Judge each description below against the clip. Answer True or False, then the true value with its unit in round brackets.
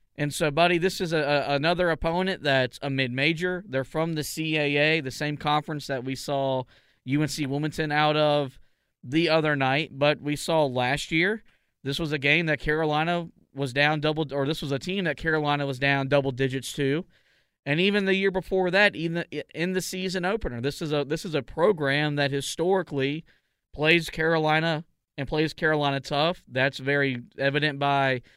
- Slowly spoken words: False (180 wpm)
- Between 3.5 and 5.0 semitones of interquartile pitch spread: False (2.8 semitones)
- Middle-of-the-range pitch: True (150 Hz)